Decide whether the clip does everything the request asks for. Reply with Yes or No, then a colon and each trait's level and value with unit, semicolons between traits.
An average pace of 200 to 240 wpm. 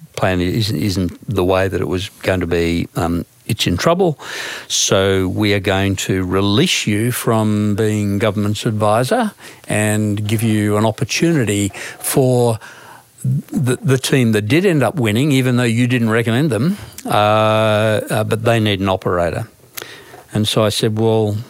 No: average, 160 wpm